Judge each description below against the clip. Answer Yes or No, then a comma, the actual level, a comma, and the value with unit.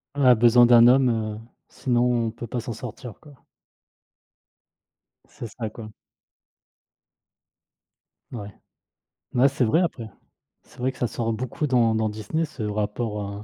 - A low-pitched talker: Yes, low, 120 Hz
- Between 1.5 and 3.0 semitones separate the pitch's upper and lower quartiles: Yes, narrow, 2.4 semitones